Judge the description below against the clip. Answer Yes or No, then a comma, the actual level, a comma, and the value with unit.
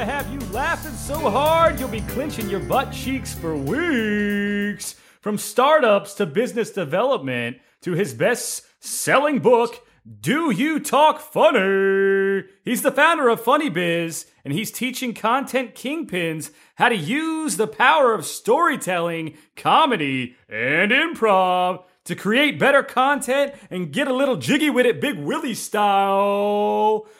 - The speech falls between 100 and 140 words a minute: Yes, slow, 135 wpm